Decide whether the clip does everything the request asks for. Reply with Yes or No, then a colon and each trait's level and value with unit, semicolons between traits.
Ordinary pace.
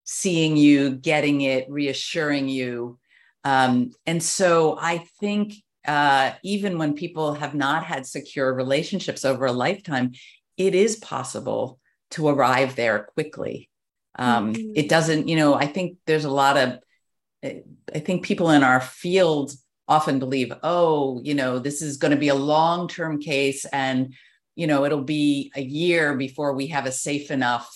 Yes: average, 160 wpm